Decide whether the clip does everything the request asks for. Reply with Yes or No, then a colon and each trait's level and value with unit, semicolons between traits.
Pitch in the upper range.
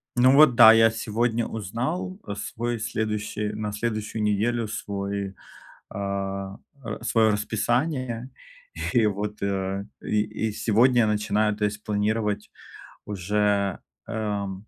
No: low, 105 Hz